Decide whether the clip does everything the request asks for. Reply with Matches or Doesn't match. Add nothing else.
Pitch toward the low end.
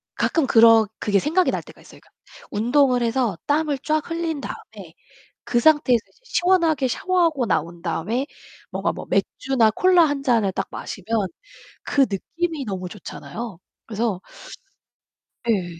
Doesn't match